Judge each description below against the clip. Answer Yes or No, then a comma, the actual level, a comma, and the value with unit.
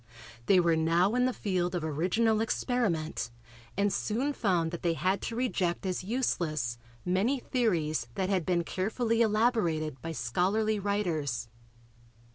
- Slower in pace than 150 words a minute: Yes, average, 140 wpm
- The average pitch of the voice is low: No, medium, 185 Hz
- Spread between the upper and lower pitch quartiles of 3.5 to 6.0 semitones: Yes, average, 5.1 semitones